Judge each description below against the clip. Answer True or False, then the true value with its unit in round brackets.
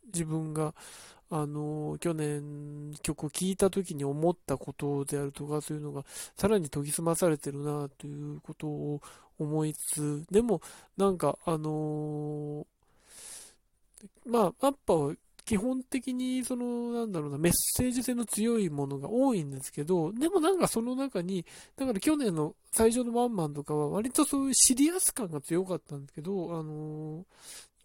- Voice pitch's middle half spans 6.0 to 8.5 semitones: True (7.2 semitones)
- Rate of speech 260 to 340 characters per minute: True (320 characters per minute)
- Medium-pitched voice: True (165 Hz)